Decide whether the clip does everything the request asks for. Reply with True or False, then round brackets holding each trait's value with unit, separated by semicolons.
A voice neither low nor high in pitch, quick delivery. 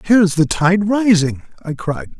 False (175 Hz; 190 wpm)